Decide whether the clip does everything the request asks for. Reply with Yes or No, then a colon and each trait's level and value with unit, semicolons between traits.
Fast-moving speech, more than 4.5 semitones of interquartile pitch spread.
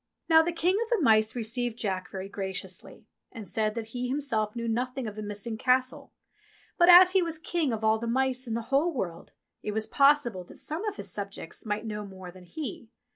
Yes: fast, 215 wpm; average, 5.0 semitones